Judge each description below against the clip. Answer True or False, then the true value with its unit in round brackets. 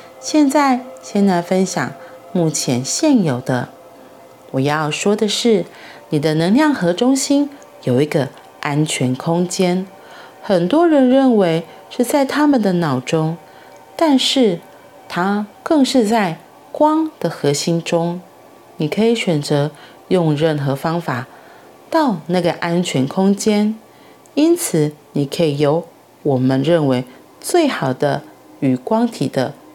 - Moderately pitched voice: True (175 Hz)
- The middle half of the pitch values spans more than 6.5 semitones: True (8.4 semitones)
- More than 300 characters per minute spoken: False (175 characters per minute)